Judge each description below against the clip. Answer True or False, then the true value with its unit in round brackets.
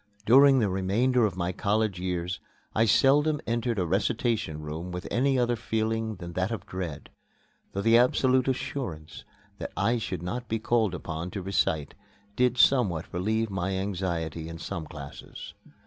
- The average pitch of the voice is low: True (100 Hz)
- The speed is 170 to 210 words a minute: False (160 wpm)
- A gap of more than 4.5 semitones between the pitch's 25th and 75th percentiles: True (5.1 semitones)